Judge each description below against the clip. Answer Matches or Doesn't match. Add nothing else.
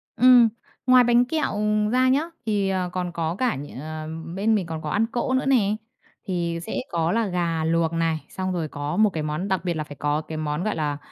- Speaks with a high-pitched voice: Doesn't match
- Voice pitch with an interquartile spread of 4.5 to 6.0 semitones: Matches